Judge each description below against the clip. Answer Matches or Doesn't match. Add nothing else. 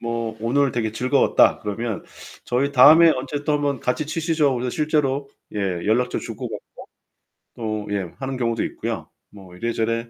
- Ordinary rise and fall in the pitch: Matches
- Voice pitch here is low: Matches